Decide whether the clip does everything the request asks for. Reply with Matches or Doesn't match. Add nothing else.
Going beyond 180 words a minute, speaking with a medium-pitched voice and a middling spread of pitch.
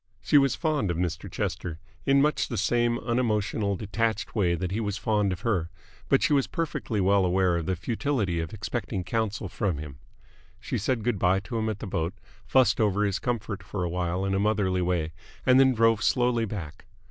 Doesn't match